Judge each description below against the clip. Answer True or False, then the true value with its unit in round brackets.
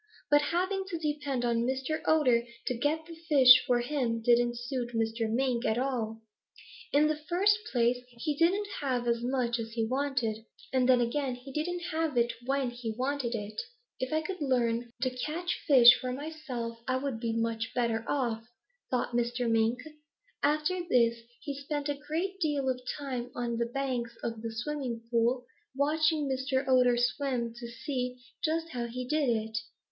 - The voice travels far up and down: False (3.7 semitones)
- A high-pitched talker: True (255 Hz)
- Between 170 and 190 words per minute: True (175 wpm)